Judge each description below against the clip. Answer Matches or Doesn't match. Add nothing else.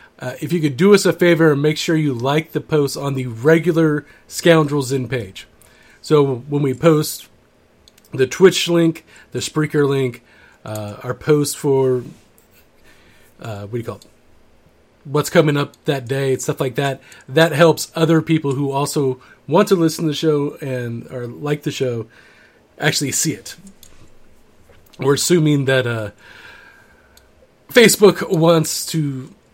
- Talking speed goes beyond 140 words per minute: Matches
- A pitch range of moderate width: Matches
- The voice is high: Doesn't match